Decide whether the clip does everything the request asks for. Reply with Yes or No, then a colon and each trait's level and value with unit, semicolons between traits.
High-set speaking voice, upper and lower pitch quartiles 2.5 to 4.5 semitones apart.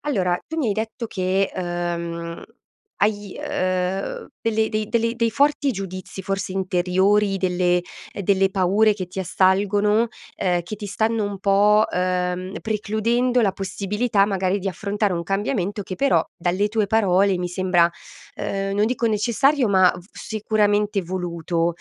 Yes: high, 195 Hz; average, 2.8 semitones